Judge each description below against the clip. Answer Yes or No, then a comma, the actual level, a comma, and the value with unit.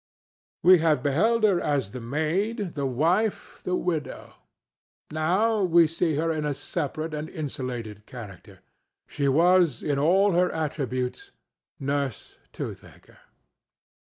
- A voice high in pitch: No, medium, 155 Hz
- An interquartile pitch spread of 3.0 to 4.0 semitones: No, average, 4.5 semitones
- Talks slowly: Yes, slow, 125 wpm